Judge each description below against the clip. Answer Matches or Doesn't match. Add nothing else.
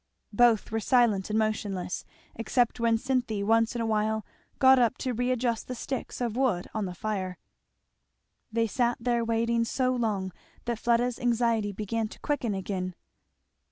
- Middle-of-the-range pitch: Doesn't match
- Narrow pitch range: Matches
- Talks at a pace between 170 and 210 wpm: Doesn't match